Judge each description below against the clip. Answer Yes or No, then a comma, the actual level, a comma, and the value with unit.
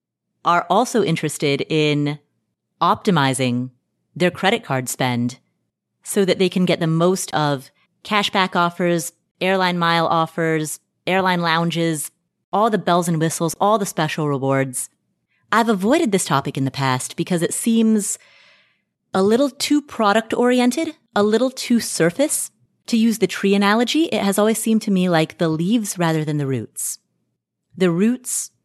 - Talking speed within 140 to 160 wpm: Yes, average, 150 wpm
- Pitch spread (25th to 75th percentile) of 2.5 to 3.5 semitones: No, average, 5.3 semitones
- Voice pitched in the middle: Yes, medium, 175 Hz